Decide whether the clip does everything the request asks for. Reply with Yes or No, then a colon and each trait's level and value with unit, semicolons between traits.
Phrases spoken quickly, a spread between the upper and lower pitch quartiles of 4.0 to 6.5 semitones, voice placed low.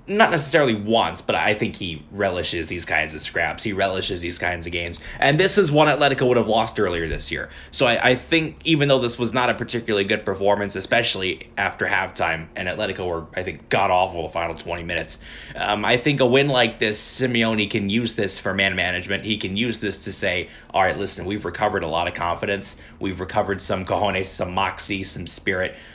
Yes: fast, 215 wpm; average, 4.7 semitones; low, 100 Hz